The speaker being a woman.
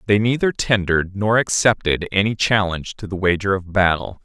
No: male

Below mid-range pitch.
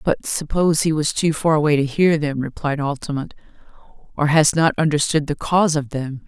No: medium, 150 Hz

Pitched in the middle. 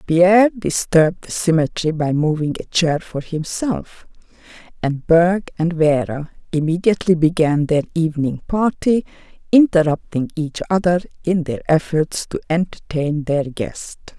Yes: medium, 165 Hz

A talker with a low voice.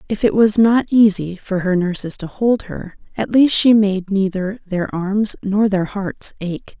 No: high, 200 Hz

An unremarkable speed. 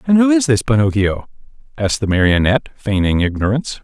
Yes: average, 155 wpm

